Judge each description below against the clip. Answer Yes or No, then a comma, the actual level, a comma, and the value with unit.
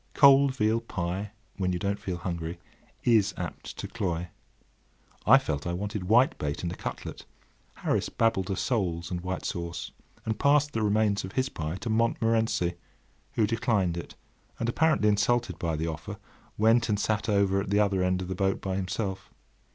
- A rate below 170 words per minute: No, average, 175 wpm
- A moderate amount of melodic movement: Yes, average, 4.1 semitones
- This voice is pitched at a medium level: No, low, 100 Hz